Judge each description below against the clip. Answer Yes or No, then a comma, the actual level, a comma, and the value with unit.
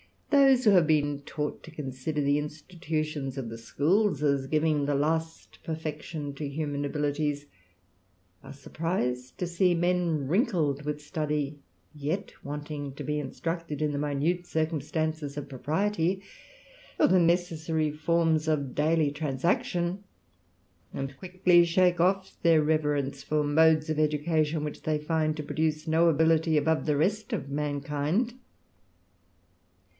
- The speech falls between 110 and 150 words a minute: Yes, slow, 135 wpm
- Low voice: No, medium, 155 Hz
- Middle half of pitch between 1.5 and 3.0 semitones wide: Yes, narrow, 2.4 semitones